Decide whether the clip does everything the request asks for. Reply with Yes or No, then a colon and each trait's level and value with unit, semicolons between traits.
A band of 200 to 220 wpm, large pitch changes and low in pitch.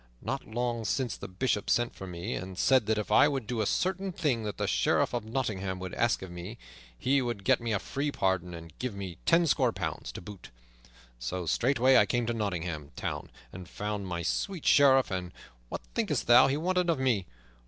Yes: fast, 205 wpm; wide, 6.0 semitones; low, 110 Hz